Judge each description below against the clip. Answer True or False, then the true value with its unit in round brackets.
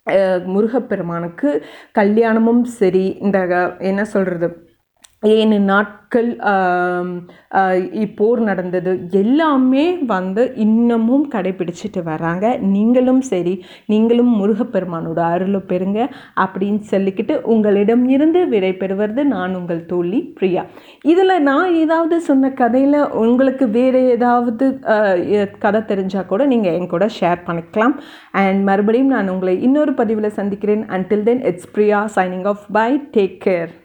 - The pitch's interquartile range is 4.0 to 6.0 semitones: True (4.5 semitones)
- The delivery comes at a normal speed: True (110 wpm)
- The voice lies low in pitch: False (210 Hz)